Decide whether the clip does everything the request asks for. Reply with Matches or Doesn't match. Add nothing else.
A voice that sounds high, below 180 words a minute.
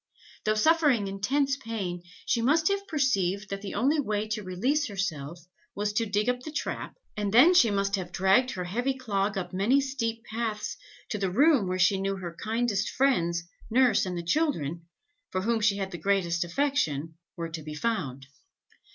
Doesn't match